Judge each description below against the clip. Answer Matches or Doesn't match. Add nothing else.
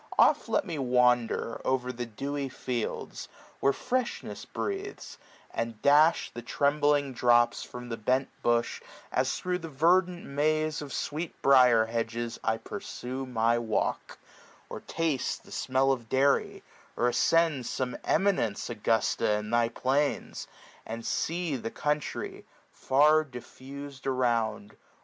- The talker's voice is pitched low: Matches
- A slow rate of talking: Matches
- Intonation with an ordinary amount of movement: Matches